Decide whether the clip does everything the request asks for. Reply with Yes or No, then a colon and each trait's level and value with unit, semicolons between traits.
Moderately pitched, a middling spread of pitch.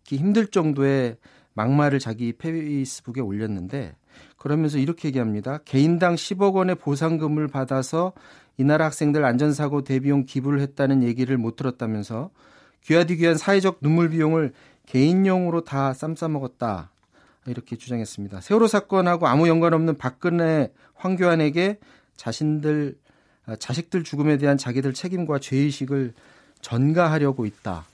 Yes: medium, 145 Hz; average, 4.2 semitones